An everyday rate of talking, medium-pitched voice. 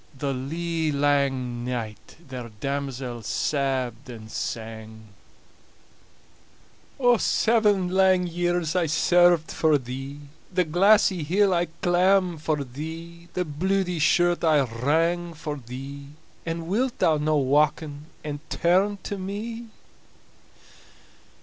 No: slow, 110 wpm; medium, 155 Hz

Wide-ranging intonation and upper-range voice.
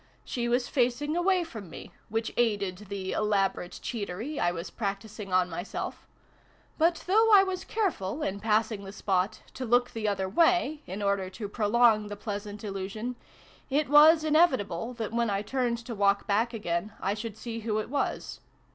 No: average, 4.3 semitones; high, 220 Hz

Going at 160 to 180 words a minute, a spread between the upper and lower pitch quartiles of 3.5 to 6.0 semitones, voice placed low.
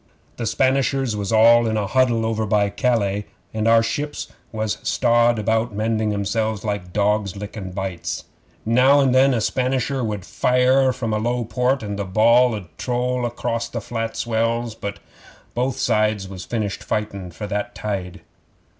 No: average, 165 wpm; average, 2.9 semitones; low, 110 Hz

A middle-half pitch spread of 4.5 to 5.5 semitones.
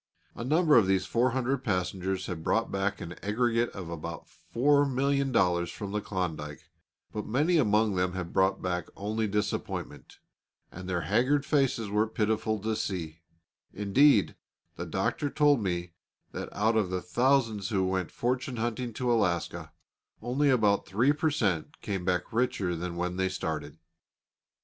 Yes: average, 5.2 semitones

